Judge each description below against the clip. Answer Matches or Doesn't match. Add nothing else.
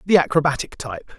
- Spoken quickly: Doesn't match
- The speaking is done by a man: Matches